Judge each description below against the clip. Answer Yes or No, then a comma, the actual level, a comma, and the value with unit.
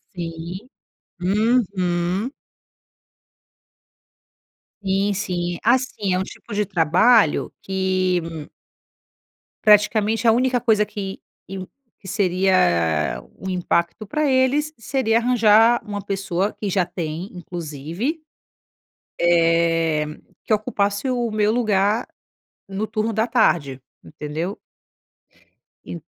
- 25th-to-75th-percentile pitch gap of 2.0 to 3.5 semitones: No, average, 4.2 semitones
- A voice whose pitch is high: Yes, high, 195 Hz